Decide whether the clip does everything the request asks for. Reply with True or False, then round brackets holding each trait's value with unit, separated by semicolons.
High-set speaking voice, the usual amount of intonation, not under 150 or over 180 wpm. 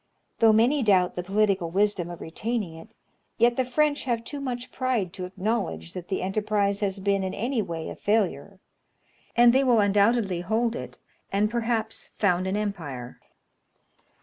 True (205 Hz; 4.0 semitones; 165 wpm)